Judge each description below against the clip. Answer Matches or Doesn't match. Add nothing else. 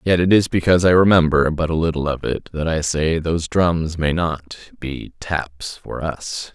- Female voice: Doesn't match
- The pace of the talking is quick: Doesn't match